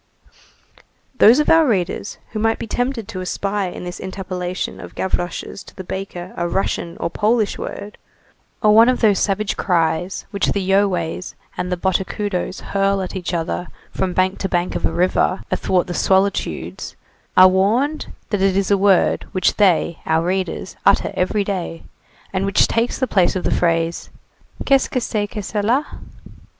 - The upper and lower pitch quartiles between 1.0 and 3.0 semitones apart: Yes, narrow, 2.5 semitones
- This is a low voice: No, high, 190 Hz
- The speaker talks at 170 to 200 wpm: Yes, average, 175 wpm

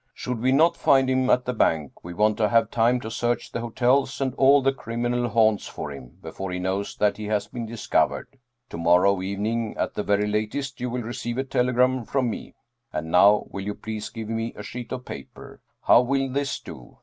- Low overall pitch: Yes, low, 115 Hz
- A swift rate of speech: Yes, fast, 215 wpm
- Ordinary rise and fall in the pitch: Yes, average, 3.5 semitones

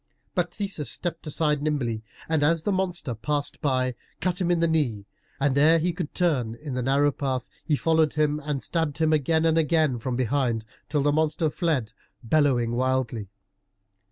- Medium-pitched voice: Yes, medium, 150 Hz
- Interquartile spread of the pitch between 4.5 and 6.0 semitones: No, average, 3.9 semitones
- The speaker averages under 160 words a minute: No, average, 180 wpm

